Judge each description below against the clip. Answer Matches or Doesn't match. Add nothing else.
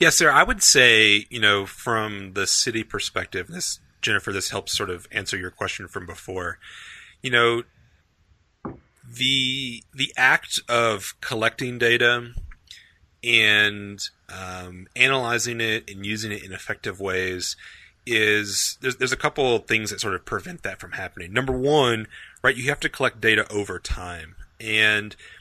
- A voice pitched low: Matches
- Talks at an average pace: Matches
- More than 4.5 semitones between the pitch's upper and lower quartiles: Doesn't match